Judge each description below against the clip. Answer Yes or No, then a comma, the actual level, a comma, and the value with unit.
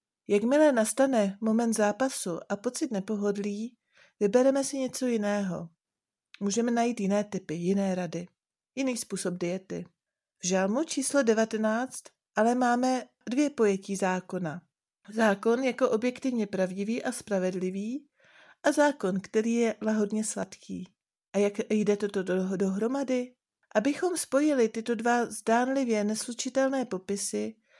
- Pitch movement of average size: Yes, average, 4.2 semitones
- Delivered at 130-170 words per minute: No, slow, 115 wpm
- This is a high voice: Yes, high, 220 Hz